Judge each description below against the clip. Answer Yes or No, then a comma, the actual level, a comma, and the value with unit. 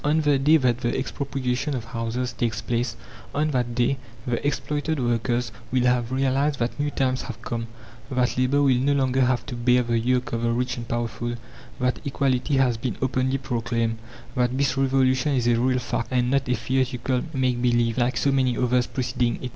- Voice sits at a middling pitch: No, low, 125 Hz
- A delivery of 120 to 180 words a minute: No, average, 195 wpm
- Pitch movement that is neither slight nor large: No, narrow, 1.9 semitones